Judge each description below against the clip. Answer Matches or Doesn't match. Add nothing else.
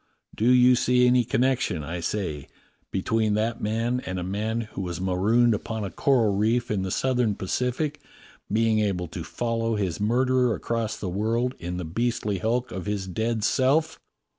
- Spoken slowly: Doesn't match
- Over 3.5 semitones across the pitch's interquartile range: Matches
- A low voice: Matches